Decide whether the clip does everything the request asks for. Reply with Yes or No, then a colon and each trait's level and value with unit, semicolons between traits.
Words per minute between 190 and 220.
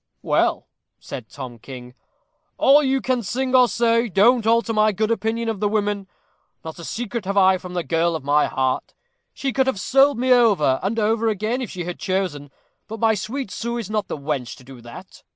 Yes: fast, 205 wpm